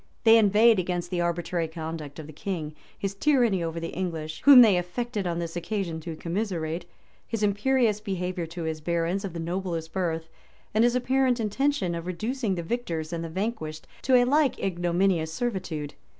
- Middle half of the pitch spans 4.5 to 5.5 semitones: Yes, average, 4.8 semitones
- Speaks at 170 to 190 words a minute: Yes, average, 180 wpm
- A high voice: No, medium, 180 Hz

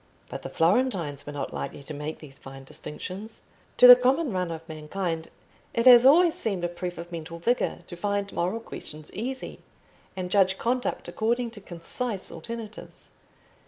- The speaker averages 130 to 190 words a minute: Yes, average, 165 wpm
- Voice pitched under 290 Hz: Yes, high, 190 Hz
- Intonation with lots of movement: Yes, wide, 6.1 semitones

